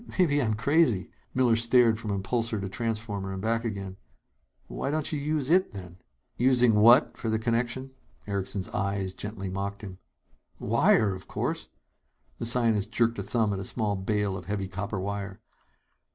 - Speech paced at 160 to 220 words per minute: Yes, average, 165 wpm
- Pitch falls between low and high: No, low, 110 Hz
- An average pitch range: Yes, average, 3.4 semitones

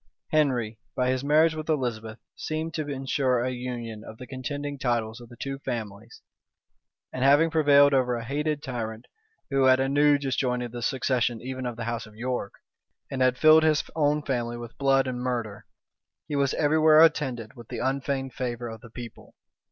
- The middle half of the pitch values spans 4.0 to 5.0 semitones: No, average, 3.1 semitones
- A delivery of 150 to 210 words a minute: Yes, average, 185 wpm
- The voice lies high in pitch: No, low, 130 Hz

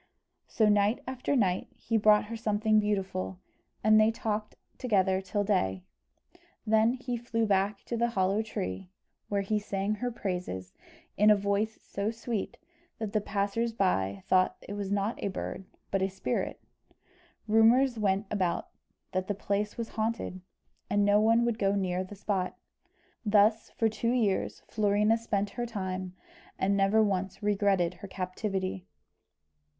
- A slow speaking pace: No, average, 155 wpm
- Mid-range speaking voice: No, high, 205 Hz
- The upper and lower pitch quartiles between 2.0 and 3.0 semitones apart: Yes, narrow, 2.4 semitones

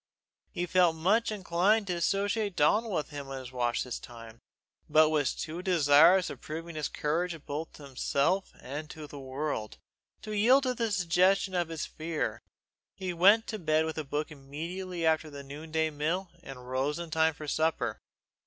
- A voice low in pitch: No, medium, 160 Hz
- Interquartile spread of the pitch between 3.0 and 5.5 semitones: Yes, average, 3.9 semitones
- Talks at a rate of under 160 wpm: No, average, 180 wpm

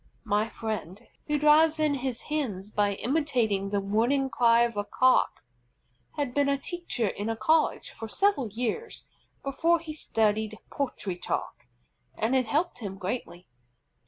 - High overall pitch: Yes, high, 240 Hz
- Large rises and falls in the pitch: Yes, wide, 5.7 semitones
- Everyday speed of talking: Yes, average, 150 wpm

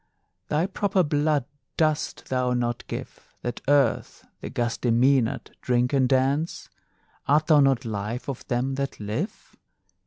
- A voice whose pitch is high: No, low, 135 Hz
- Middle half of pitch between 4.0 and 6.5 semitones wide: No, average, 3.4 semitones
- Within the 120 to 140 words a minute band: Yes, slow, 135 wpm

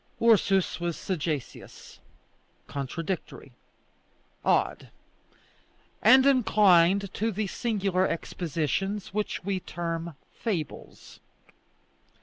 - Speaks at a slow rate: Yes, slow, 75 wpm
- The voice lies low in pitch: No, high, 190 Hz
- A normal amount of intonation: Yes, average, 3.7 semitones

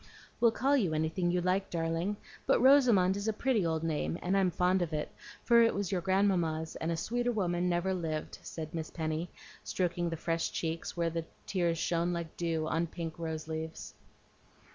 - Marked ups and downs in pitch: No, average, 2.8 semitones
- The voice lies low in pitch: No, medium, 175 Hz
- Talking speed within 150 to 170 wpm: No, average, 190 wpm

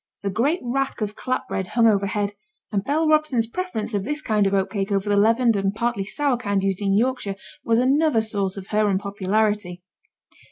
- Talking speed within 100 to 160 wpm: No, average, 195 wpm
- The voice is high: Yes, high, 215 Hz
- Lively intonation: No, average, 3.8 semitones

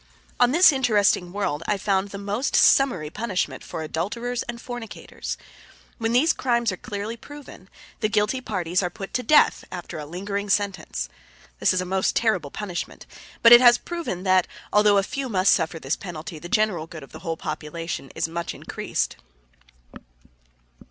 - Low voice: No, high, 200 Hz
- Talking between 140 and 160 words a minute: No, average, 170 wpm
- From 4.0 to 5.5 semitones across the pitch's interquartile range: Yes, average, 5.1 semitones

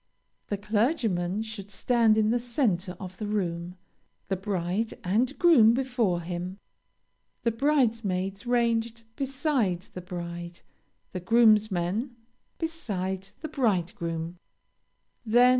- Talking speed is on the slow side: Yes, slow, 105 wpm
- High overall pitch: Yes, high, 210 Hz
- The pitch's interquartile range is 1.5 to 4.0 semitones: No, average, 4.7 semitones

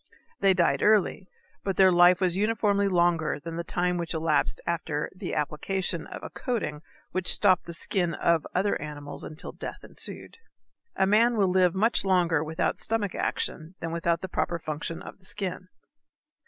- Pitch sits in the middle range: Yes, medium, 180 Hz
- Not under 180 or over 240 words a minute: No, average, 170 wpm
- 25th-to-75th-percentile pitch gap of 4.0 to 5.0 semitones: No, average, 2.8 semitones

